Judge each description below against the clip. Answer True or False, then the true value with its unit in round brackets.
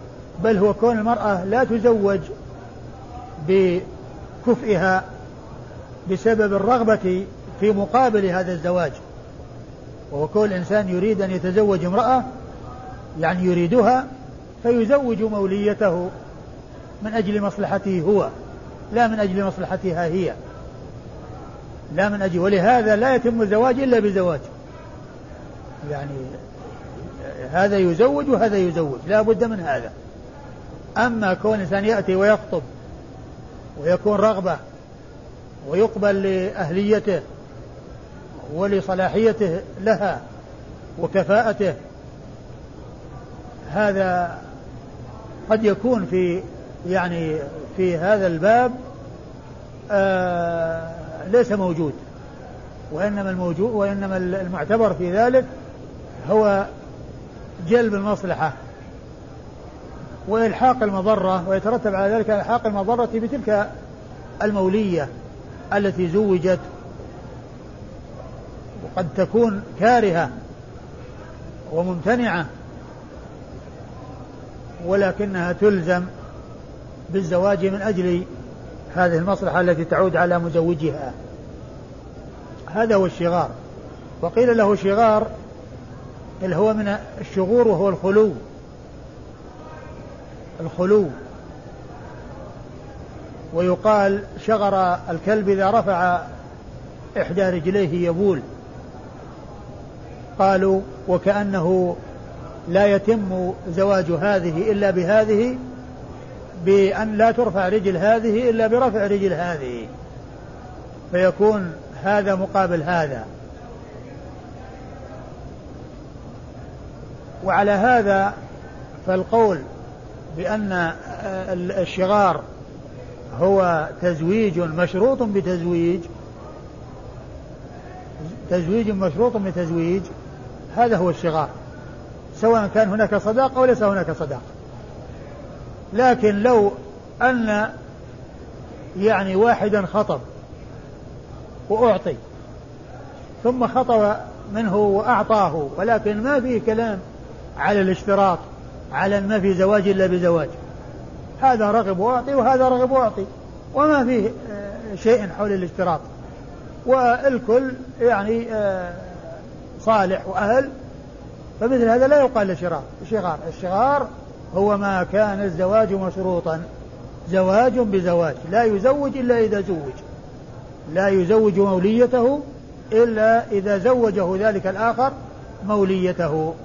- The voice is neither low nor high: False (195 Hz)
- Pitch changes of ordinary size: True (3.7 semitones)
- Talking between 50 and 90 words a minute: True (80 wpm)